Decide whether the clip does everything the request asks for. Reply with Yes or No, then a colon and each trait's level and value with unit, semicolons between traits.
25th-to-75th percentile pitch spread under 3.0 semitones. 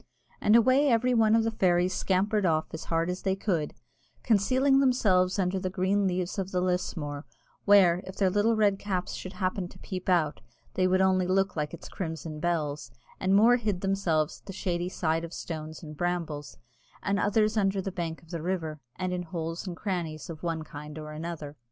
No: average, 3.3 semitones